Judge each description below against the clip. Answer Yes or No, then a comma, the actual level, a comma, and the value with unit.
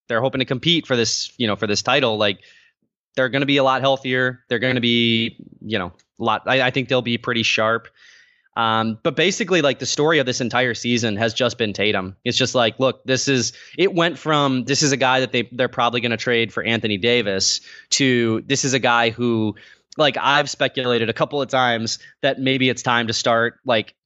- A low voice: Yes, low, 125 Hz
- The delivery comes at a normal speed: No, fast, 220 wpm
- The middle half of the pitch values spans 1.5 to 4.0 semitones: Yes, average, 2.8 semitones